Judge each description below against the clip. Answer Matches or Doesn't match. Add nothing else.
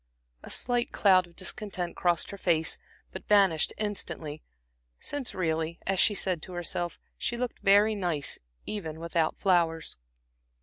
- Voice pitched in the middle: Matches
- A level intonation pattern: Doesn't match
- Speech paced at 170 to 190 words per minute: Doesn't match